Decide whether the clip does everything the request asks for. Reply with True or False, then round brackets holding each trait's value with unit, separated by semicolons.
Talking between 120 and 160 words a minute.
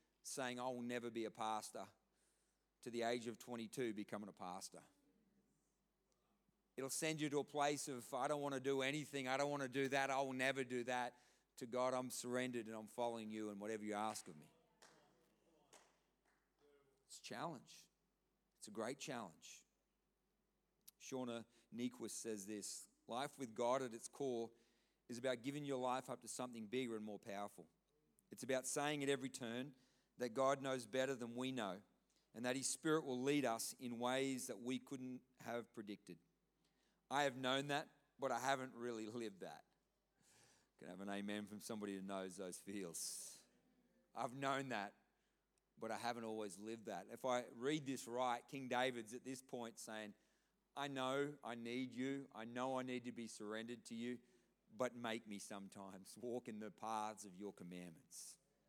False (180 wpm)